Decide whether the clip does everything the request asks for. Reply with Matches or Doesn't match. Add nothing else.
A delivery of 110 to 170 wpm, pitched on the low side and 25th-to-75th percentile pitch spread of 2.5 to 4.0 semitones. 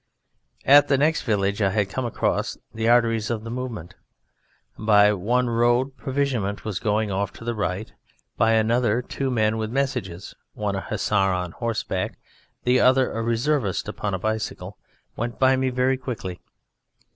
Matches